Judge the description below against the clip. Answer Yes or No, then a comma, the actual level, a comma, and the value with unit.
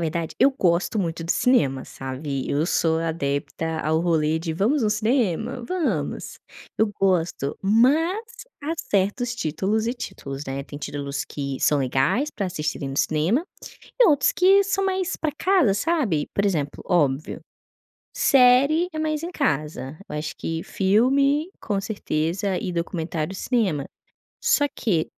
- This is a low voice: No, high, 190 Hz